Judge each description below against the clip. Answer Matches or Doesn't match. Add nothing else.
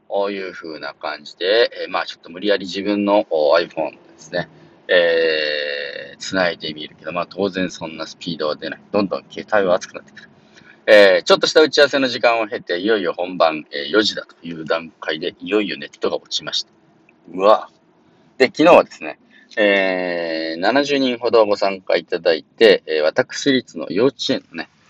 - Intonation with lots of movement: Matches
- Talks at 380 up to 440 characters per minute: Doesn't match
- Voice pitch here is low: Matches